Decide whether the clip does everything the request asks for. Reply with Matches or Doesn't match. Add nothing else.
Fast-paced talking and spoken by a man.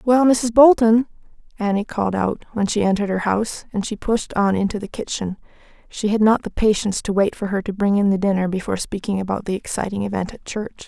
Doesn't match